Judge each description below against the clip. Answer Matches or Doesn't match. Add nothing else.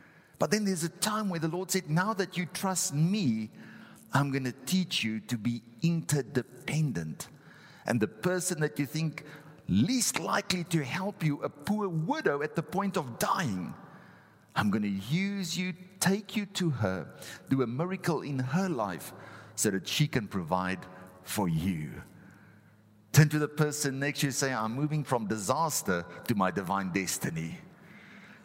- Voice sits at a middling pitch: Matches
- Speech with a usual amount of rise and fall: Doesn't match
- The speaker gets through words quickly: Doesn't match